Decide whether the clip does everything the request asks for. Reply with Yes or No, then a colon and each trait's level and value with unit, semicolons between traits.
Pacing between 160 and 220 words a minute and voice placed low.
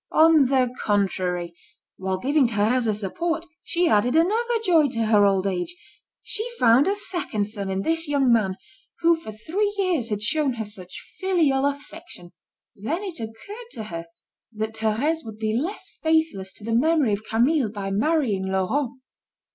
No: average, 165 wpm; high, 240 Hz